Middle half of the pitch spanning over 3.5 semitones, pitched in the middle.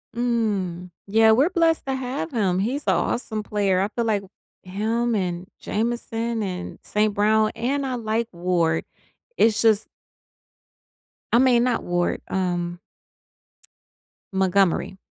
No: average, 3.9 semitones; high, 215 Hz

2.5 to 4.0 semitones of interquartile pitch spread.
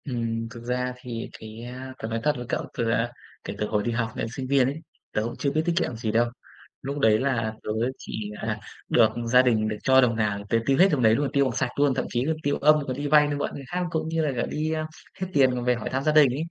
Yes: average, 3.5 semitones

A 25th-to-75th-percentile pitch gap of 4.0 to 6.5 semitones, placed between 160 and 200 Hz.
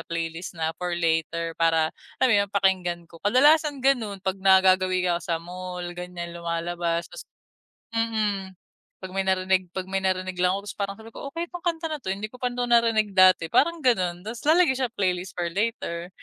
Yes: average, 4.5 semitones; high, 190 Hz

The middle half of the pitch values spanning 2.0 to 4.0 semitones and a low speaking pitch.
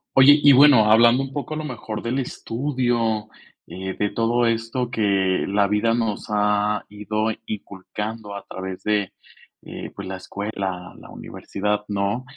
Yes: average, 2.9 semitones; low, 110 Hz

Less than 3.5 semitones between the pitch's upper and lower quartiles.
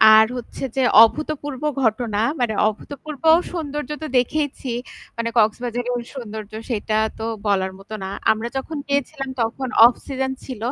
No: average, 4.1 semitones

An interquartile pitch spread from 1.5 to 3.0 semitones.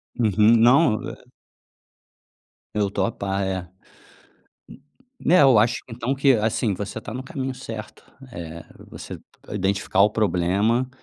No: average, 3.8 semitones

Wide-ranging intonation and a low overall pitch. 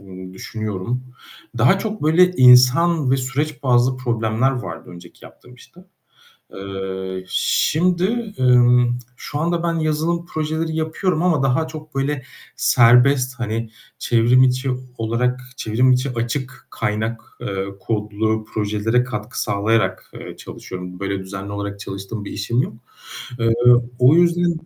Yes: wide, 6.1 semitones; low, 125 Hz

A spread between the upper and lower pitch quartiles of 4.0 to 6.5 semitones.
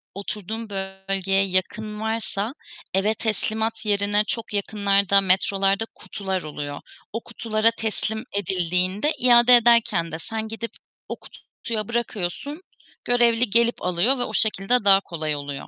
No: average, 3.0 semitones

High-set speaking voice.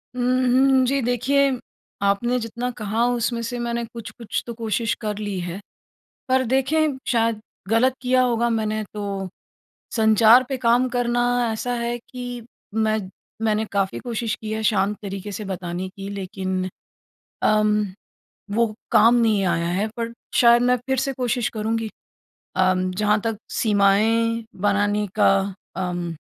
Yes: high, 225 Hz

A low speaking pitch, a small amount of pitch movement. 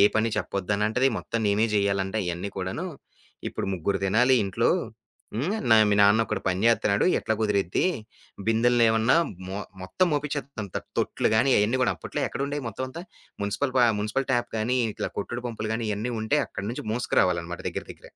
No: low, 110 Hz; average, 3.5 semitones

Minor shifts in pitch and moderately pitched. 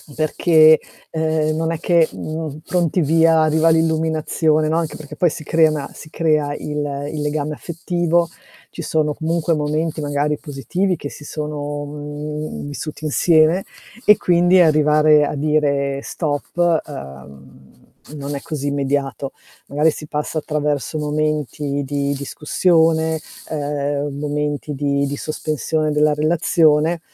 Yes: narrow, 1.7 semitones; medium, 150 Hz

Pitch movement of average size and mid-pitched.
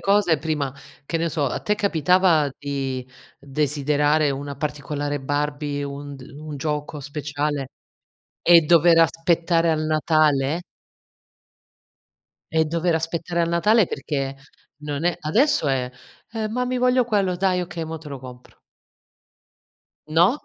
Yes: average, 3.1 semitones; medium, 155 Hz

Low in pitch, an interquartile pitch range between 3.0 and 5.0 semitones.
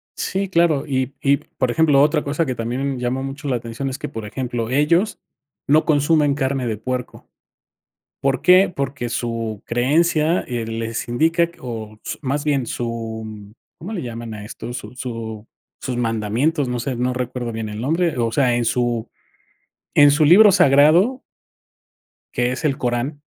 Yes: low, 130 Hz; average, 4.1 semitones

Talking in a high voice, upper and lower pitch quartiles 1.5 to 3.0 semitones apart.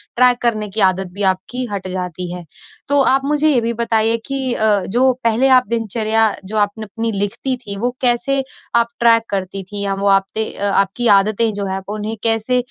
No: high, 220 Hz; average, 3.5 semitones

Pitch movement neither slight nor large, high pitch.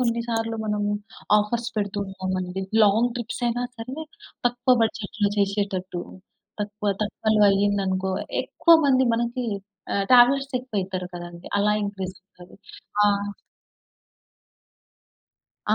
Yes: average, 3.6 semitones; high, 210 Hz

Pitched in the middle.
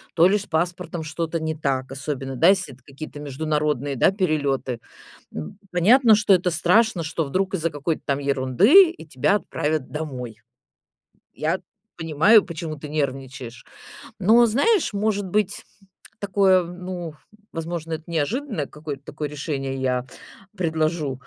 Yes: medium, 160 Hz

